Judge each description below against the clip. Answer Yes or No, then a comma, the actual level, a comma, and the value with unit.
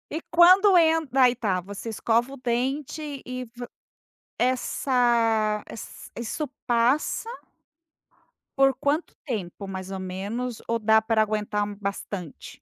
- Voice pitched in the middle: No, high, 235 Hz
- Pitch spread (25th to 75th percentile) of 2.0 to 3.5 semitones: No, average, 4.2 semitones